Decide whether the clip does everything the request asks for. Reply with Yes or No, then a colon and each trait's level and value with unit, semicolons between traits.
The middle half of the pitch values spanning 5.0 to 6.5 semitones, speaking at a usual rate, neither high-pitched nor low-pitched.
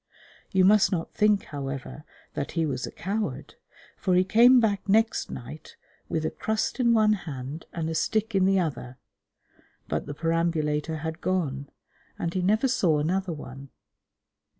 Yes: average, 5.3 semitones; average, 160 wpm; medium, 170 Hz